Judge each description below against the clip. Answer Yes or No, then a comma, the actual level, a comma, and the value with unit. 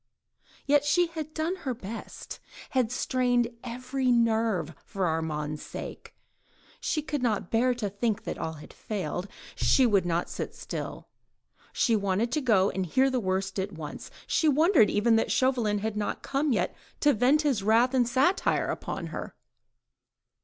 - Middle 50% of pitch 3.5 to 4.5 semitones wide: No, average, 5.1 semitones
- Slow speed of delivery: No, average, 160 wpm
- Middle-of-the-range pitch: No, high, 230 Hz